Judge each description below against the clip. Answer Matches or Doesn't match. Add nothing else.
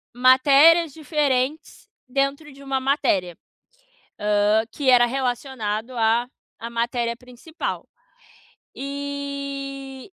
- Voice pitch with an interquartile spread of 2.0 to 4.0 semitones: Matches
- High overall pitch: Matches